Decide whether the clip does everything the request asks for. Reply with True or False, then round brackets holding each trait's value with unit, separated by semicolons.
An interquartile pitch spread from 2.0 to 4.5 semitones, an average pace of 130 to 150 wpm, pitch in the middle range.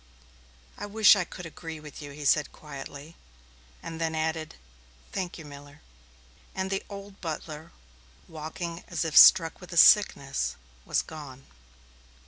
True (3.1 semitones; 140 wpm; 160 Hz)